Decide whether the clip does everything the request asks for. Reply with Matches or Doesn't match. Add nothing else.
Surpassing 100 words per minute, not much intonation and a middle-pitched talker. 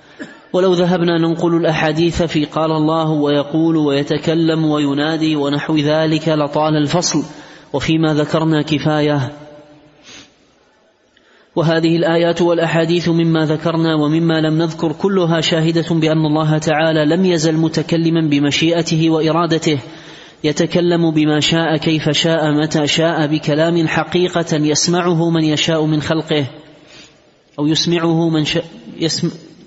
Matches